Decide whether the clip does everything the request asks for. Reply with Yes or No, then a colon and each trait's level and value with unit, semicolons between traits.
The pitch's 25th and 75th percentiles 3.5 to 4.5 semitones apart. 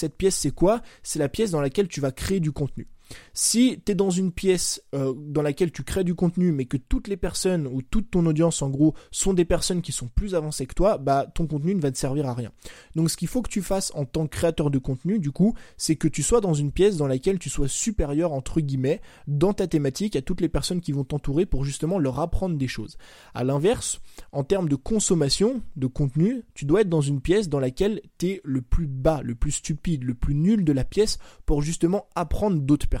No: average, 5.0 semitones